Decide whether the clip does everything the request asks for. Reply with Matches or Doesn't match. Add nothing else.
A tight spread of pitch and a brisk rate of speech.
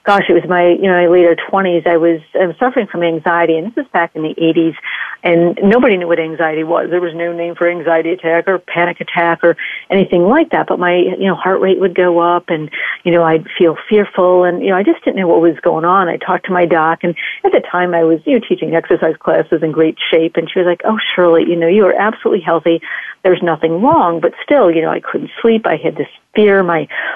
Matches